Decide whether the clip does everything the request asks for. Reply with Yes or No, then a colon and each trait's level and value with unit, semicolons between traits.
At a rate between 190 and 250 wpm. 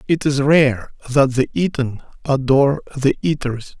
No: average, 140 wpm